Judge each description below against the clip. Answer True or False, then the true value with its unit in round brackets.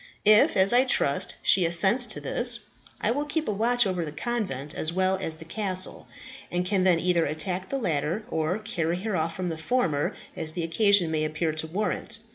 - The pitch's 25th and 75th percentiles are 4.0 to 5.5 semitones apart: True (4.9 semitones)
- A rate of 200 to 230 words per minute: True (205 wpm)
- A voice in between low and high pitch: True (180 Hz)